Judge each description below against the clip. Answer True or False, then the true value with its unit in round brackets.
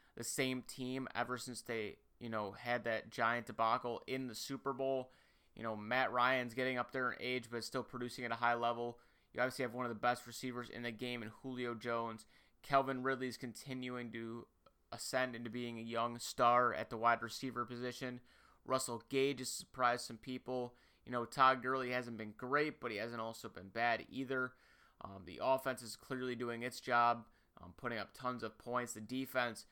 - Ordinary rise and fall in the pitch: False (1.5 semitones)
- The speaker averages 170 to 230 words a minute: True (195 wpm)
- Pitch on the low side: True (125 Hz)